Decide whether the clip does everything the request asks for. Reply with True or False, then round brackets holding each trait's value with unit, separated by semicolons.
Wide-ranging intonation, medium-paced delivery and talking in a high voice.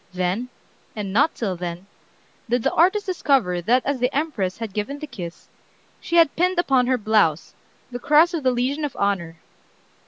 True (7.2 semitones; 180 wpm; 245 Hz)